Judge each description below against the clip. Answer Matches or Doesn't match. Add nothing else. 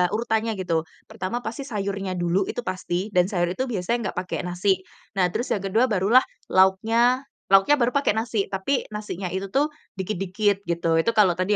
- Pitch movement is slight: Doesn't match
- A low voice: Doesn't match